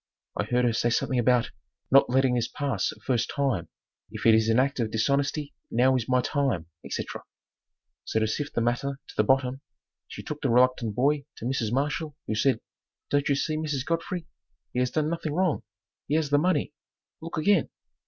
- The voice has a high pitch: No, low, 135 Hz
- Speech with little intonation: No, average, 3.5 semitones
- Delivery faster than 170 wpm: Yes, average, 195 wpm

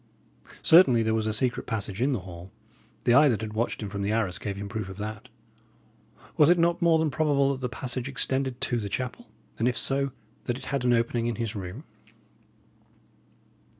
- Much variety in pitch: No, average, 4.2 semitones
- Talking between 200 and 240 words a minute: Yes, fast, 205 wpm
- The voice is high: No, low, 120 Hz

